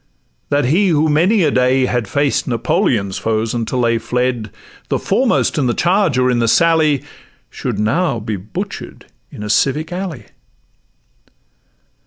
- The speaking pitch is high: No, low, 130 Hz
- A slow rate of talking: No, average, 150 wpm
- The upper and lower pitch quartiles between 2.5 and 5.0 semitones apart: No, wide, 5.5 semitones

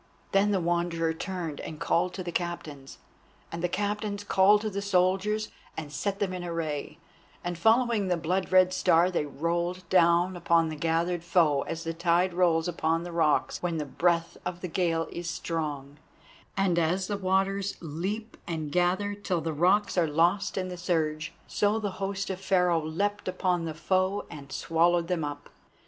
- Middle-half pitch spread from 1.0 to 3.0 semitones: Yes, narrow, 2.6 semitones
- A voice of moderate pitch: Yes, medium, 175 Hz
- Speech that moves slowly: No, average, 180 wpm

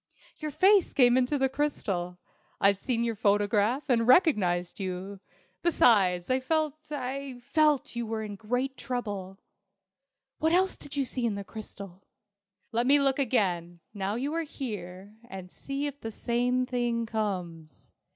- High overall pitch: Yes, high, 235 Hz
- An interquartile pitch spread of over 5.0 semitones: Yes, wide, 5.5 semitones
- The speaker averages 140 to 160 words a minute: Yes, average, 155 wpm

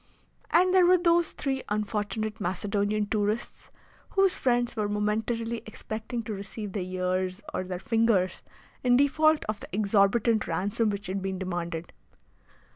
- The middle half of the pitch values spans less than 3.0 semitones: No, average, 3.3 semitones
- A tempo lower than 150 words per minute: Yes, average, 140 wpm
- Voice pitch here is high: Yes, high, 210 Hz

